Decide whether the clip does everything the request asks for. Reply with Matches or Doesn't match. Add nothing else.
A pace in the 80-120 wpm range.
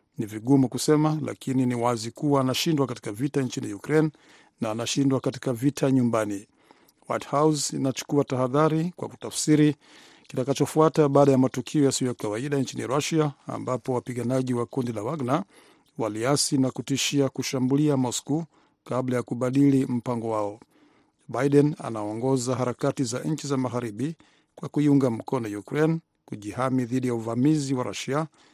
Doesn't match